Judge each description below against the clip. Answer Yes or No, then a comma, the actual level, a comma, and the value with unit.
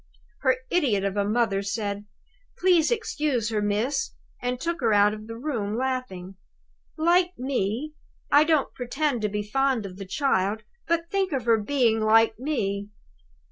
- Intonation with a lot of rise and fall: Yes, wide, 5.8 semitones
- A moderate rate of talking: Yes, average, 165 wpm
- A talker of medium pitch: No, high, 235 Hz